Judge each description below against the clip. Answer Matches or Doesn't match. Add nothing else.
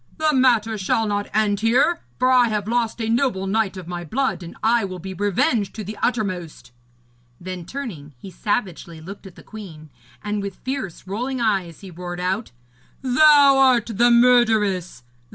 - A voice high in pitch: Matches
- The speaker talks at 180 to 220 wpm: Doesn't match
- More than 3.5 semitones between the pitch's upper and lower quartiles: Matches